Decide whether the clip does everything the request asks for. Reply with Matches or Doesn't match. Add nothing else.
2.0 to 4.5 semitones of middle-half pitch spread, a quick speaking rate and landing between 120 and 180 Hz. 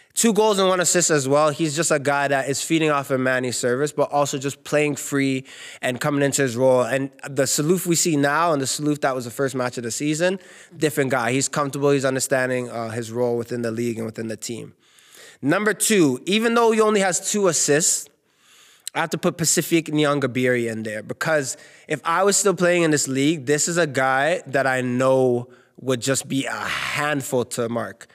Matches